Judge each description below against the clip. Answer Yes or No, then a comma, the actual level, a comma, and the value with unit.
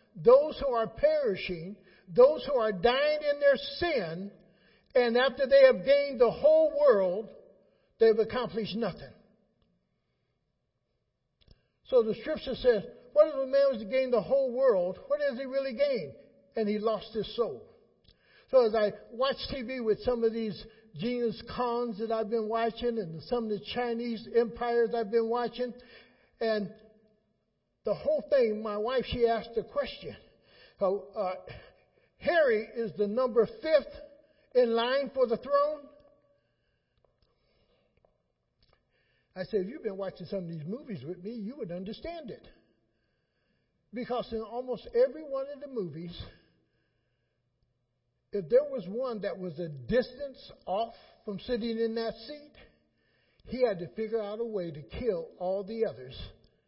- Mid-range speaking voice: No, high, 235 Hz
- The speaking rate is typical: Yes, average, 150 wpm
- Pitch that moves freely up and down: No, average, 4.3 semitones